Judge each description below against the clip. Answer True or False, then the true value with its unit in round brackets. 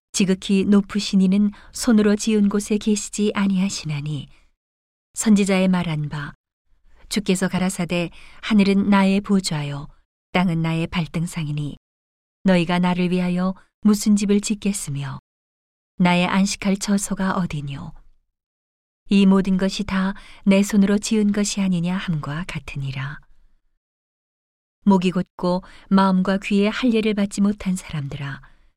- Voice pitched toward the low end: False (185 Hz)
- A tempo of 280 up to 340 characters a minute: False (260 characters per minute)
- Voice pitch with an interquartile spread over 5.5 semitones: False (5.1 semitones)